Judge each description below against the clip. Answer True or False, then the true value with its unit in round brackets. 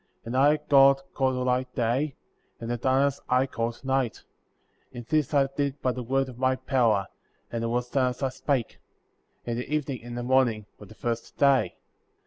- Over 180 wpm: True (200 wpm)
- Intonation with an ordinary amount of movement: False (2.2 semitones)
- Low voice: True (130 Hz)